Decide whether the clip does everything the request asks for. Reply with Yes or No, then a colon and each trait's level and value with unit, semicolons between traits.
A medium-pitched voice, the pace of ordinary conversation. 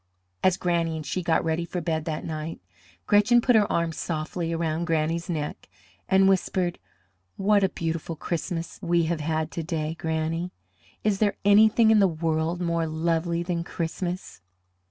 Yes: medium, 170 Hz; average, 160 wpm